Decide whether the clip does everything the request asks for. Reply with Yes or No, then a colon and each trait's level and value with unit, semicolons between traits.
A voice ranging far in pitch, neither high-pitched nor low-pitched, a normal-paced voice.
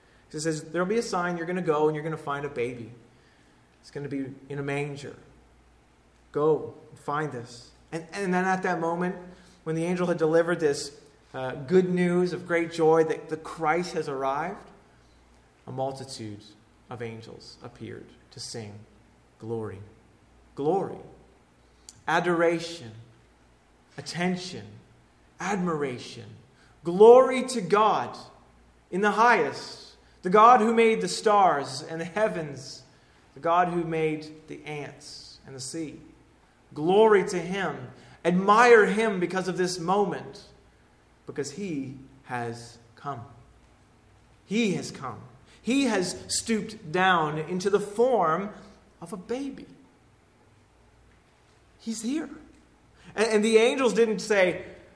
No: wide, 7.1 semitones; medium, 160 Hz; slow, 130 wpm